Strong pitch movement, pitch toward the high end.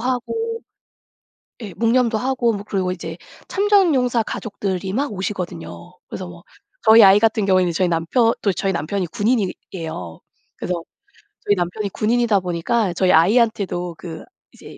No: average, 4.6 semitones; high, 200 Hz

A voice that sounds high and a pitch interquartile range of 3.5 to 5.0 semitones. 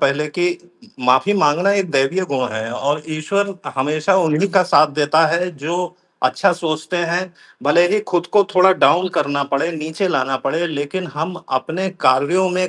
No: medium, 160 Hz; average, 4.2 semitones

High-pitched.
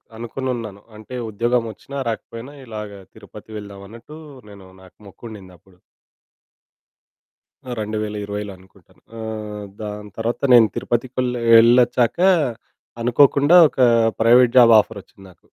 No: low, 110 Hz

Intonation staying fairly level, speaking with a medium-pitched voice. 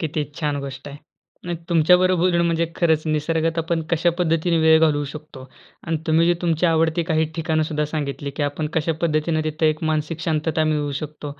Yes: narrow, 1.5 semitones; medium, 160 Hz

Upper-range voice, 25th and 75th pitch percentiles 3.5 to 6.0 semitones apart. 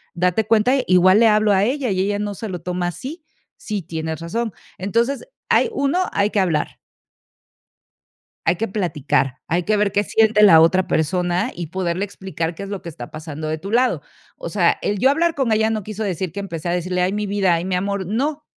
Yes: high, 195 Hz; average, 3.9 semitones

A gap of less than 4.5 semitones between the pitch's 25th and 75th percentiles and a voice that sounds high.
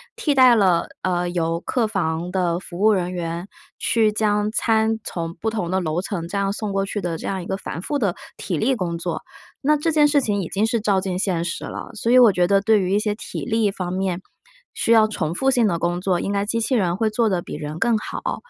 Yes: average, 4.0 semitones; high, 195 Hz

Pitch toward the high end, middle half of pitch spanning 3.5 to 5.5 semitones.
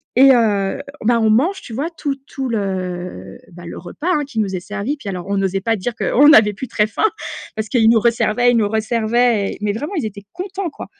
Yes: high, 220 Hz; average, 4.5 semitones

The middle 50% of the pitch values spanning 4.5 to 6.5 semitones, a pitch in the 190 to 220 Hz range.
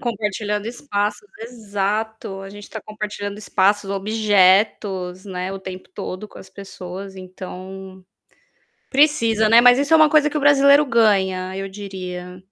No: average, 3.0 semitones; high, 205 Hz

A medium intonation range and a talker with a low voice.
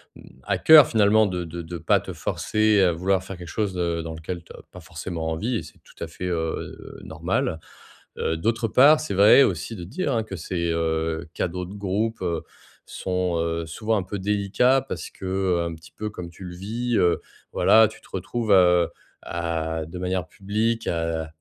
Yes: average, 4.3 semitones; very low, 90 Hz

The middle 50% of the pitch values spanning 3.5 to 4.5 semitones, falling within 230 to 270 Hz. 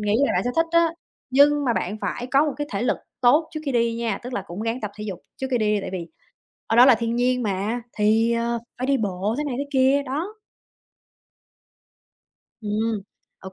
Yes: average, 4.2 semitones; high, 235 Hz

